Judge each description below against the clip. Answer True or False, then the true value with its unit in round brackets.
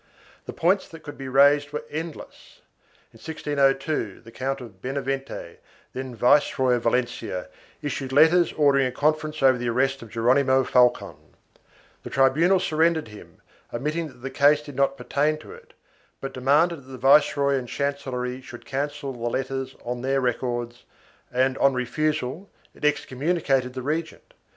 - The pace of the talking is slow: False (155 wpm)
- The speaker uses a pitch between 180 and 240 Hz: False (135 Hz)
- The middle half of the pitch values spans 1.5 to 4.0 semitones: True (2.9 semitones)